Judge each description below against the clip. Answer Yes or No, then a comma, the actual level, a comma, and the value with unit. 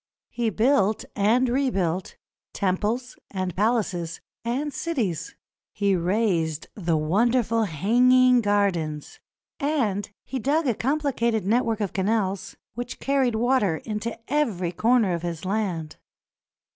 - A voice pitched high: Yes, high, 215 Hz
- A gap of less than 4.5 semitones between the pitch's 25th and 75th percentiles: No, average, 4.8 semitones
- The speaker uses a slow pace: Yes, slow, 115 wpm